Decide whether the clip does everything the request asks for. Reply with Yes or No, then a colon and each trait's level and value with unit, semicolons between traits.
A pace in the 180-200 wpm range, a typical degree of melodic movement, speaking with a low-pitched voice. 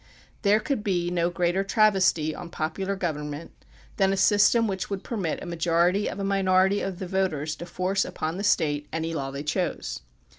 No: average, 190 wpm; average, 3.2 semitones; medium, 185 Hz